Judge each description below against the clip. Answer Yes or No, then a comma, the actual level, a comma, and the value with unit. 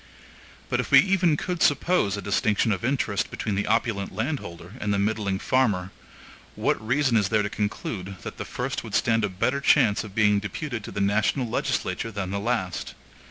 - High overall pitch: No, low, 105 Hz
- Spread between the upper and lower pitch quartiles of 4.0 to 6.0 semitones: No, average, 3.6 semitones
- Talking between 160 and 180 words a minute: No, average, 190 wpm